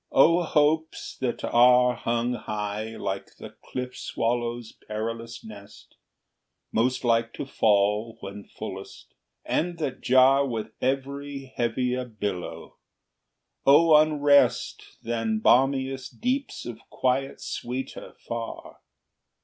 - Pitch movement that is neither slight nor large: Yes, average, 3.2 semitones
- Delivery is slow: Yes, slow, 105 wpm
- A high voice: No, low, 125 Hz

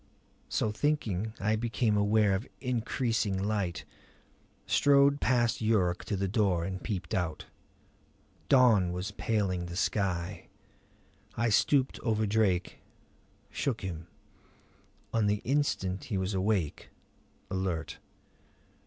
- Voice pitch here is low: Yes, low, 105 Hz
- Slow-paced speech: Yes, slow, 110 wpm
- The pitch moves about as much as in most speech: Yes, average, 3.5 semitones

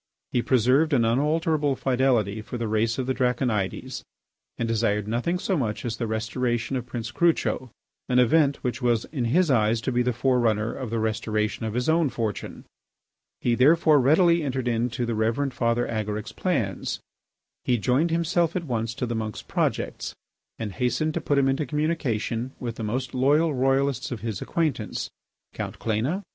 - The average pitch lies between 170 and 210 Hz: No, low, 125 Hz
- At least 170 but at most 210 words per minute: Yes, average, 180 wpm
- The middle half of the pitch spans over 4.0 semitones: No, average, 3.6 semitones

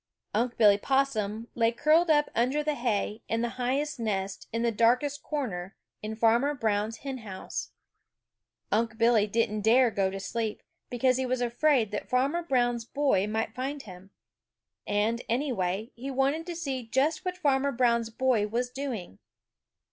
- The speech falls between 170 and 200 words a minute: No, average, 160 wpm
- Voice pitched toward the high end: Yes, high, 235 Hz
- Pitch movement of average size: Yes, average, 3.8 semitones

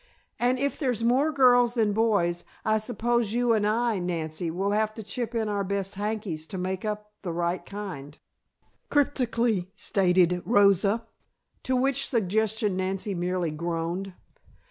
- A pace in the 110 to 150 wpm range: Yes, average, 145 wpm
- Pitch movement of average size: Yes, average, 4.1 semitones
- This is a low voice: No, high, 210 Hz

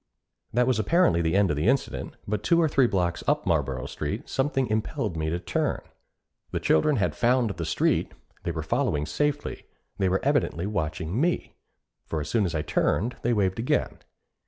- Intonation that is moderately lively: No, wide, 7.4 semitones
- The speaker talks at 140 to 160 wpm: No, average, 185 wpm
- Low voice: Yes, low, 100 Hz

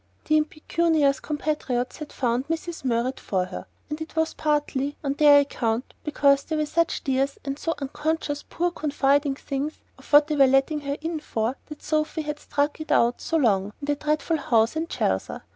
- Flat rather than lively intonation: Yes, narrow, 2.3 semitones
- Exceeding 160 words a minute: Yes, average, 190 wpm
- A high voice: Yes, very high, 290 Hz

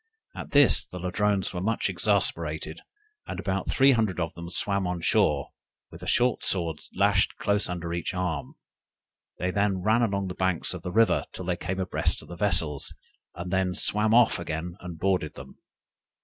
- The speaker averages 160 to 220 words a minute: Yes, average, 180 wpm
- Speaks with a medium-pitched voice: No, very low, 90 Hz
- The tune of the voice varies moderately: Yes, average, 3.0 semitones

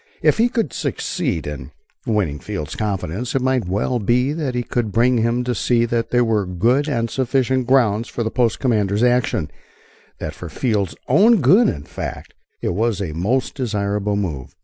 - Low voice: Yes, low, 115 Hz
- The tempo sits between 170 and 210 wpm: Yes, average, 180 wpm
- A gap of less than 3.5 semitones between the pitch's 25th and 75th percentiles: No, average, 3.9 semitones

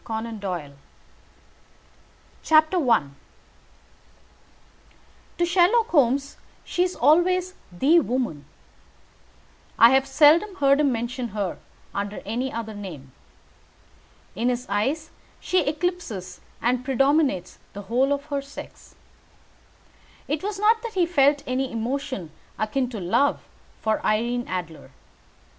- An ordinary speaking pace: No, slow, 115 wpm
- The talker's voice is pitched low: No, very high, 265 Hz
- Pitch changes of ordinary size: No, wide, 6.2 semitones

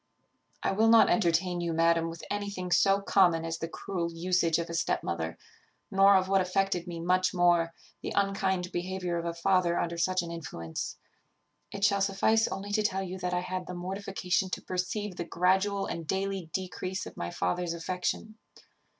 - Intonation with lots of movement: No, narrow, 2.4 semitones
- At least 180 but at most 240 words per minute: Yes, average, 185 wpm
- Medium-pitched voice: Yes, medium, 180 Hz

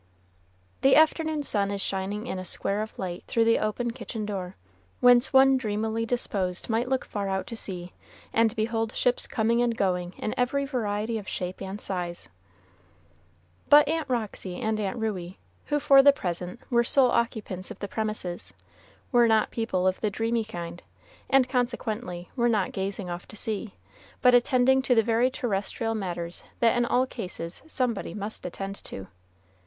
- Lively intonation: No, average, 4.2 semitones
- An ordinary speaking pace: Yes, average, 170 wpm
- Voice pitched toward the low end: No, high, 220 Hz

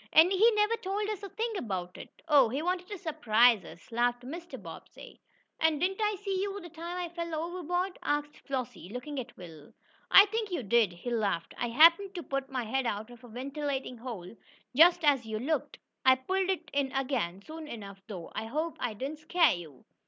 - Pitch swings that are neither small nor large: No, wide, 7.1 semitones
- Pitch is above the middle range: Yes, very high, 285 Hz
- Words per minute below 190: No, fast, 205 wpm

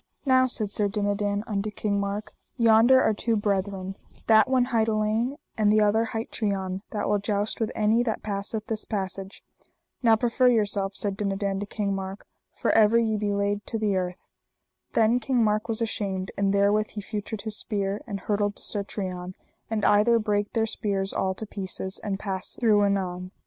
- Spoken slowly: No, average, 185 wpm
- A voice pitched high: Yes, high, 210 Hz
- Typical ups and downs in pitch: No, narrow, 1.9 semitones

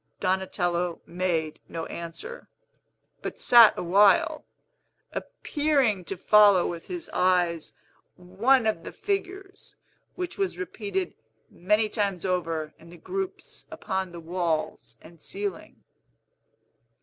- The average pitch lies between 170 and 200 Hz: Yes, high, 190 Hz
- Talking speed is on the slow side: Yes, slow, 110 wpm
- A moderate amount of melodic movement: No, wide, 6.7 semitones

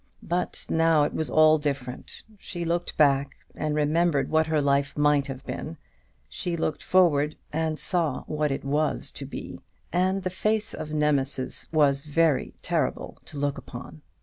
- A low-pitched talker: No, medium, 150 Hz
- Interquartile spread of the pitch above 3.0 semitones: No, narrow, 2.6 semitones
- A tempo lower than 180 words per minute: Yes, average, 160 wpm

